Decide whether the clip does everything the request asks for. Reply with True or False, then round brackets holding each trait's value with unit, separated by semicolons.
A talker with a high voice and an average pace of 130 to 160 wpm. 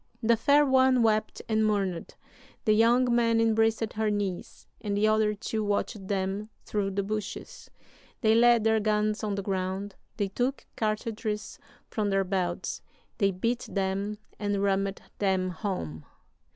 True (210 Hz; 150 wpm)